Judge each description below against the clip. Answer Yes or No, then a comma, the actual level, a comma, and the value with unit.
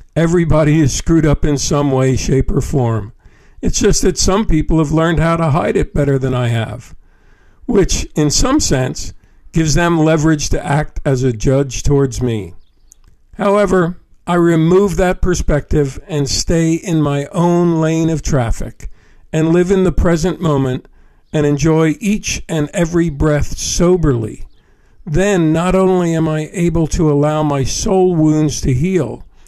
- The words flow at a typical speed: Yes, average, 160 wpm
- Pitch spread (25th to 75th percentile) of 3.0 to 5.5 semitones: Yes, average, 3.6 semitones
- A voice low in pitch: No, medium, 155 Hz